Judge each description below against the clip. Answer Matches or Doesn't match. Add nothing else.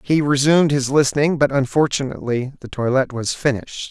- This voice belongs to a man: Matches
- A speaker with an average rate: Matches